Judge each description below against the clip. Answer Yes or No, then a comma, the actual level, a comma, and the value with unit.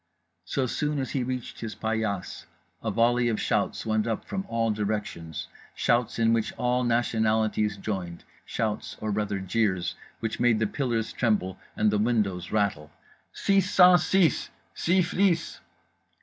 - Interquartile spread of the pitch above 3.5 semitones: No, average, 2.8 semitones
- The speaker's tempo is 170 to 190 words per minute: No, average, 145 wpm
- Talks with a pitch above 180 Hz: No, low, 115 Hz